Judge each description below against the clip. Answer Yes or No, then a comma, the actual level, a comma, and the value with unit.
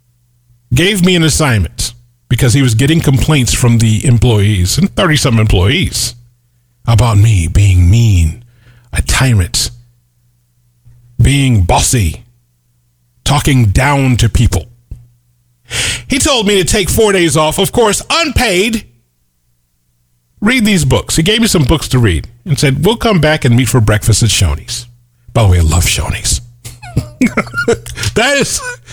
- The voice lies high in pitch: No, low, 120 Hz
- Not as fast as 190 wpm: Yes, average, 140 wpm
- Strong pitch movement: No, average, 5.0 semitones